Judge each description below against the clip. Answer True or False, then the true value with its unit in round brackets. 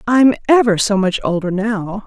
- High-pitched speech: True (210 Hz)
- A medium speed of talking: True (175 wpm)